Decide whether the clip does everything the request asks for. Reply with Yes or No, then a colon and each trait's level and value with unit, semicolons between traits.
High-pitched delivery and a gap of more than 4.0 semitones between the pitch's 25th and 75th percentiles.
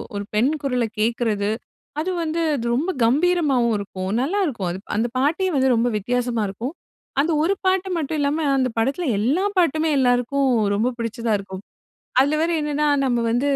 Yes: very high, 260 Hz; average, 5.2 semitones